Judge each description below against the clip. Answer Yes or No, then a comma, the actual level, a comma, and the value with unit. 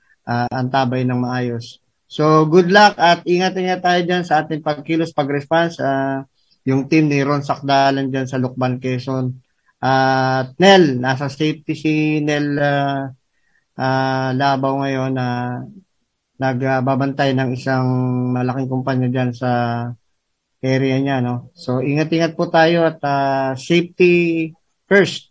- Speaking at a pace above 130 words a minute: Yes, average, 140 wpm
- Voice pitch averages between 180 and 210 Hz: No, low, 135 Hz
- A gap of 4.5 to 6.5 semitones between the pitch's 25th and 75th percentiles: No, average, 3.4 semitones